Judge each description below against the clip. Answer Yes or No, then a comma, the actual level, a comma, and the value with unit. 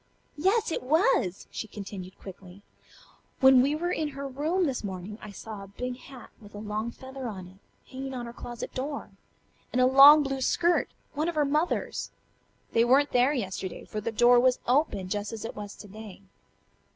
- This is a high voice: Yes, very high, 250 Hz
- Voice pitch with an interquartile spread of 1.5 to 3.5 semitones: No, average, 5.3 semitones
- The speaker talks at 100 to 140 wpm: No, average, 190 wpm